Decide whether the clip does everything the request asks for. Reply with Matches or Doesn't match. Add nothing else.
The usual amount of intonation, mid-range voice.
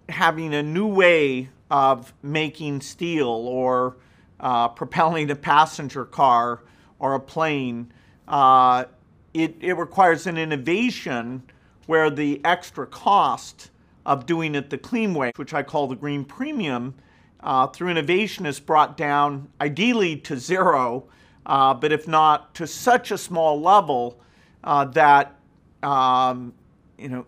Matches